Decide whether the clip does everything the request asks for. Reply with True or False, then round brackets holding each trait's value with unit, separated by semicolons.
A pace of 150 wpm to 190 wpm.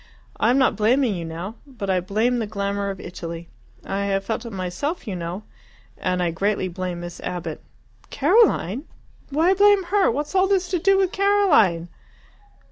True (175 wpm)